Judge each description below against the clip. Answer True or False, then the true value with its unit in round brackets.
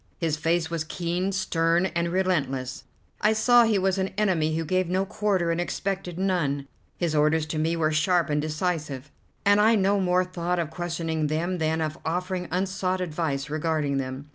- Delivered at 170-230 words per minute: True (180 wpm)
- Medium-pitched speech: True (170 Hz)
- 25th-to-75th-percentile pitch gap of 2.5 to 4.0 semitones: True (3.1 semitones)